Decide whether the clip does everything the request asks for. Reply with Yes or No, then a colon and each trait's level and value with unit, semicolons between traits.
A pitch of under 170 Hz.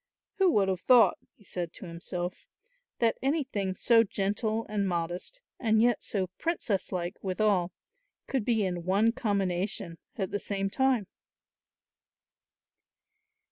No: high, 200 Hz